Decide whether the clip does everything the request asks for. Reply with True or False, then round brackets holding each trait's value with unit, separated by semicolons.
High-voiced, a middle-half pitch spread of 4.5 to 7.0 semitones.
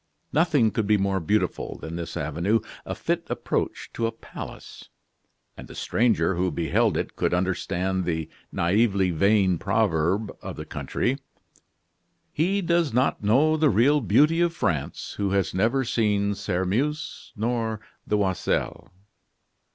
False (105 Hz; 4.9 semitones)